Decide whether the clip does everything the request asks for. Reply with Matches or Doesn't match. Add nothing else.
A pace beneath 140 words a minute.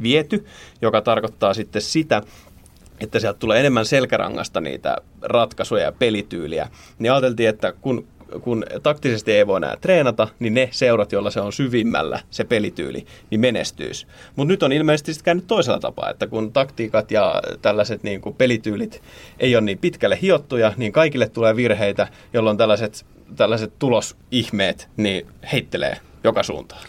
Doesn't match